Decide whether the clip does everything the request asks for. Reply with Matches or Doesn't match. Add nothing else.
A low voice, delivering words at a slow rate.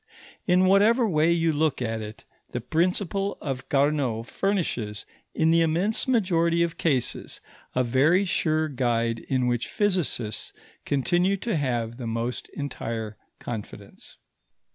Doesn't match